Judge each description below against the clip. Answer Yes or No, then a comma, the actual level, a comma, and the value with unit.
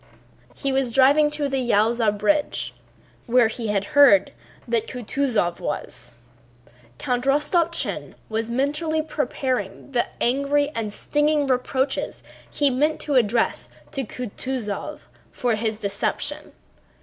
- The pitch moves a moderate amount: Yes, average, 4.3 semitones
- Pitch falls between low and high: No, very high, 255 Hz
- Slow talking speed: Yes, slow, 115 wpm